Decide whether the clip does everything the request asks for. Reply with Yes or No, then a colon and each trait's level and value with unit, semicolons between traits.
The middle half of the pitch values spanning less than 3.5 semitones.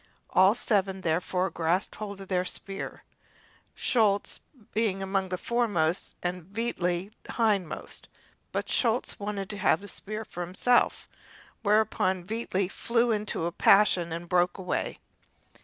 Yes: average, 2.9 semitones